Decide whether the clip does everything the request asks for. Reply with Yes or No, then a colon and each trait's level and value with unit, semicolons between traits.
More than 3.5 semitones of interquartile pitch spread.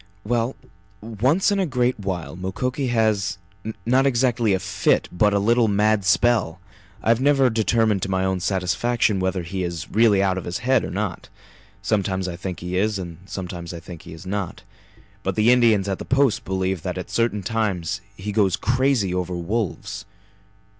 Yes: average, 4.0 semitones